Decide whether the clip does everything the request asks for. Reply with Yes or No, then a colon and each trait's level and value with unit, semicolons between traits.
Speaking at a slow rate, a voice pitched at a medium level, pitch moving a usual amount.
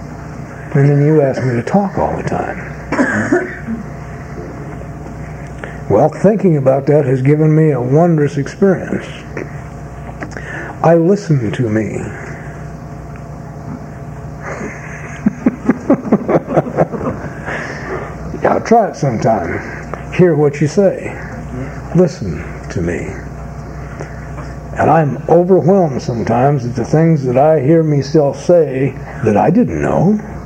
Yes: slow, 100 wpm; medium, 145 Hz; average, 3.1 semitones